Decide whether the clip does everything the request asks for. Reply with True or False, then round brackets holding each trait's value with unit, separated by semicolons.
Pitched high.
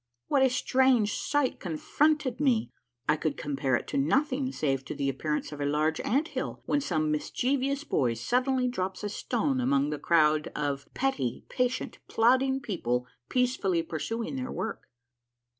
True (220 Hz)